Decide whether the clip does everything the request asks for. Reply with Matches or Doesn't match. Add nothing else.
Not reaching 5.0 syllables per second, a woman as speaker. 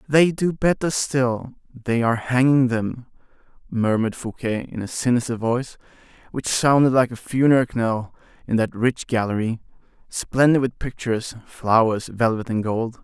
Doesn't match